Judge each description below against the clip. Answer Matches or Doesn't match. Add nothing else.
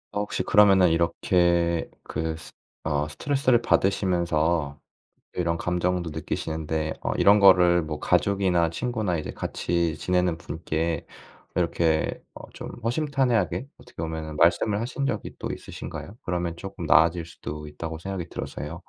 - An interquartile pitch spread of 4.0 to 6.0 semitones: Doesn't match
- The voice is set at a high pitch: Doesn't match